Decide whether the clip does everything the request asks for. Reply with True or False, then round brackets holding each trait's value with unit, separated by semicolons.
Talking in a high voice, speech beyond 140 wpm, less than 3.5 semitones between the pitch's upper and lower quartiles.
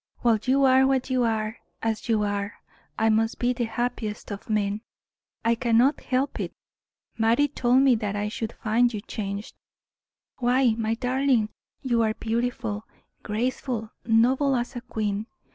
True (230 Hz; 160 wpm; 2.6 semitones)